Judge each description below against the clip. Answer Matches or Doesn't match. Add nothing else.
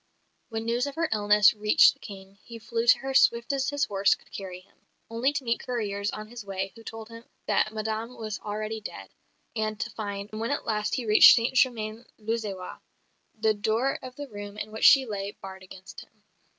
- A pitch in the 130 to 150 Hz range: Doesn't match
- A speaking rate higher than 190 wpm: Matches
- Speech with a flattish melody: Matches